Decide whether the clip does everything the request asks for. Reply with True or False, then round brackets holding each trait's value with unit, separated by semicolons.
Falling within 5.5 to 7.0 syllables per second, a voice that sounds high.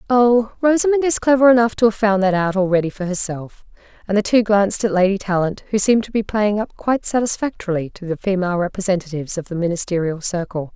True (6.4 syllables/s; 205 Hz)